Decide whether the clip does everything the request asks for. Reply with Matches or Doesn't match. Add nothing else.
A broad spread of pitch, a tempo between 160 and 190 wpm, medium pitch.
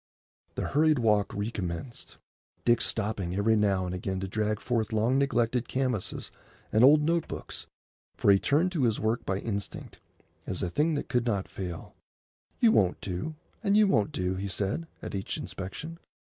Doesn't match